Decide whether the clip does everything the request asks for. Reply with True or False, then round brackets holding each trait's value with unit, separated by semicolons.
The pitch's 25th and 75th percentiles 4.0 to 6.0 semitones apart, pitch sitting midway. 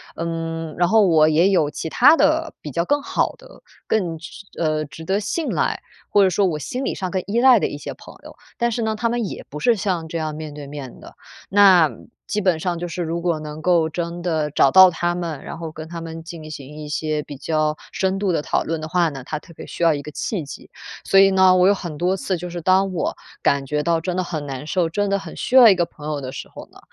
False (3.6 semitones; 170 Hz)